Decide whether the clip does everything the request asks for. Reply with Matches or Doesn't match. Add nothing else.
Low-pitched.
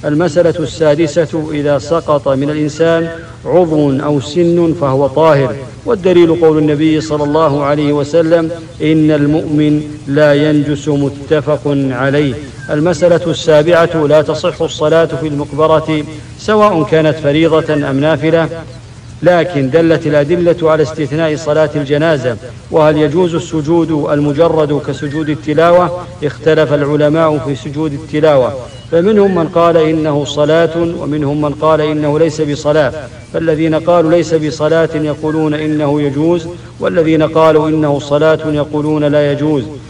Doesn't match